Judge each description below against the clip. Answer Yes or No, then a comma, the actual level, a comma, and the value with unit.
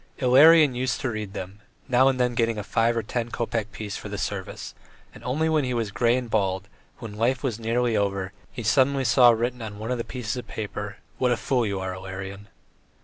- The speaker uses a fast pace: Yes, fast, 220 wpm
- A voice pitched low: Yes, low, 115 Hz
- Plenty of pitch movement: No, average, 3.4 semitones